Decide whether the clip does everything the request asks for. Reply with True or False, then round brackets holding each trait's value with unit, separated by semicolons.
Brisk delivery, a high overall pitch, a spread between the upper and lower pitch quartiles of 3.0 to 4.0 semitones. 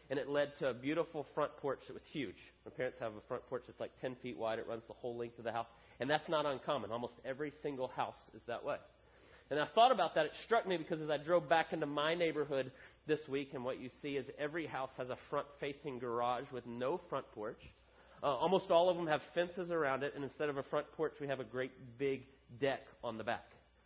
False (250 wpm; 135 Hz; 3.3 semitones)